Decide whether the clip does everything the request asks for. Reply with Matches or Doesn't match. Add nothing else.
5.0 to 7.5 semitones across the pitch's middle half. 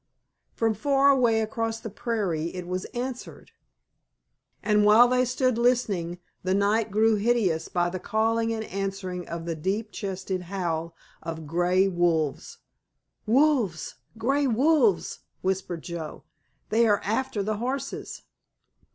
Doesn't match